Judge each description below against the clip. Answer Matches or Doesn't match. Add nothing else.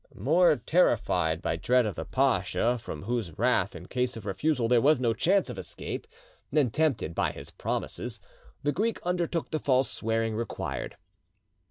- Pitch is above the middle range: Doesn't match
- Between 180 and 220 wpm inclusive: Doesn't match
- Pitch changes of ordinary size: Doesn't match